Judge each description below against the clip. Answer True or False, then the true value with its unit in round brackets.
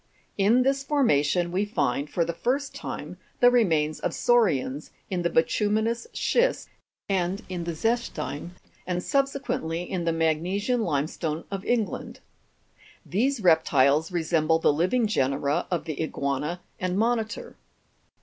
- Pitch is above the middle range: False (180 Hz)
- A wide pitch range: True (6.1 semitones)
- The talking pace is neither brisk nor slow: False (130 wpm)